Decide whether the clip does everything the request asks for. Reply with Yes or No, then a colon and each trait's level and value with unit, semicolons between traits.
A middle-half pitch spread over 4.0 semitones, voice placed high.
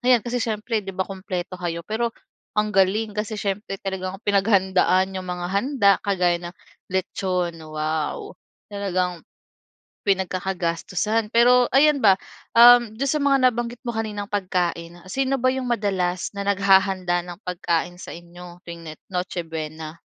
No: average, 3.7 semitones; high, 195 Hz